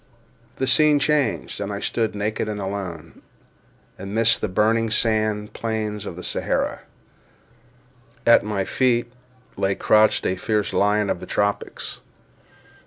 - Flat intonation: Yes, narrow, 2.1 semitones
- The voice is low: Yes, low, 105 Hz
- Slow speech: Yes, slow, 125 wpm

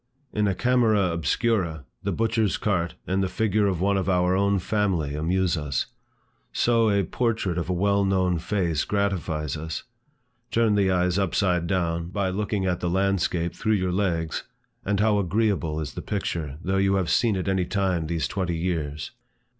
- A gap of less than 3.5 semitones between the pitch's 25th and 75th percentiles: Yes, average, 3.0 semitones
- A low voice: Yes, very low, 95 Hz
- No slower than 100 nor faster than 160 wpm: No, average, 175 wpm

